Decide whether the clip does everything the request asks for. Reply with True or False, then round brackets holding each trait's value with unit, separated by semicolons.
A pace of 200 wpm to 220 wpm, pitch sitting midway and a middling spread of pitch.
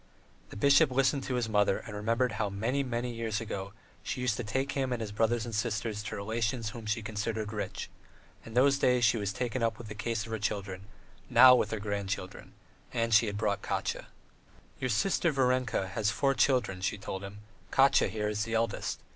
False (205 wpm; 110 Hz; 3.1 semitones)